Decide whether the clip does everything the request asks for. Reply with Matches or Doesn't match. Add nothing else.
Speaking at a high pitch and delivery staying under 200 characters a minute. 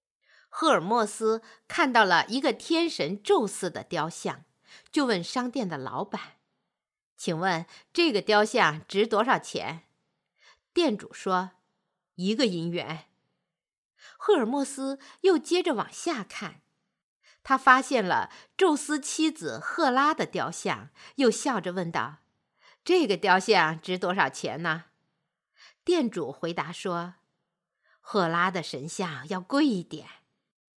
Matches